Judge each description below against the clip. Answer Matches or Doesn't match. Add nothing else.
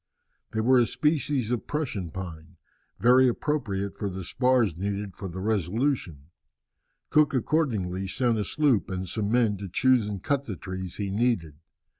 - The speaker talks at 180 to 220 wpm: Doesn't match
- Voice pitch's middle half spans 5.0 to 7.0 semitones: Matches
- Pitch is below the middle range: Matches